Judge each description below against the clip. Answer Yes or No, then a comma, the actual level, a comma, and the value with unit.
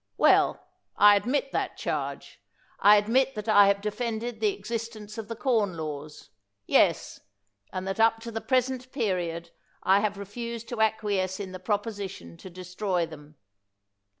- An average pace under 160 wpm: No, average, 165 wpm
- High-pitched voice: Yes, high, 205 Hz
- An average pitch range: Yes, average, 3.7 semitones